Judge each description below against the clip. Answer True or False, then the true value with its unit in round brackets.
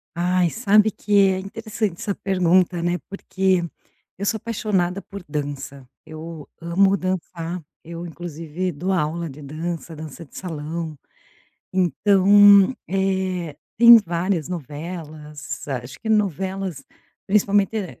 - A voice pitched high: False (180 Hz)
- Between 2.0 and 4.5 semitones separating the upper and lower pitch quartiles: True (3.5 semitones)